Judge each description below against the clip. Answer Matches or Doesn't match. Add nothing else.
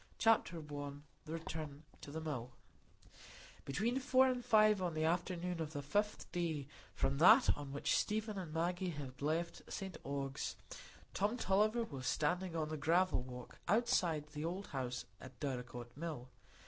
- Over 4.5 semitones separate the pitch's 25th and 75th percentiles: Matches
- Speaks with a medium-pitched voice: Matches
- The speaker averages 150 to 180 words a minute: Matches